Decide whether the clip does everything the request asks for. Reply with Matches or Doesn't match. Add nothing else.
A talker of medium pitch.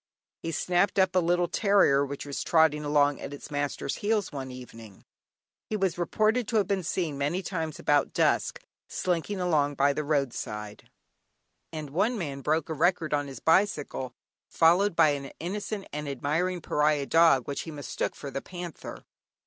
Matches